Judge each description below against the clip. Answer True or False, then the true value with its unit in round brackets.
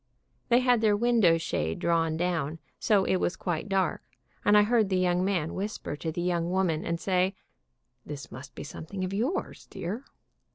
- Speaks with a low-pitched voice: False (185 Hz)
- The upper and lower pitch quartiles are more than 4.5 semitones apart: False (3.7 semitones)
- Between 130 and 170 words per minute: False (180 wpm)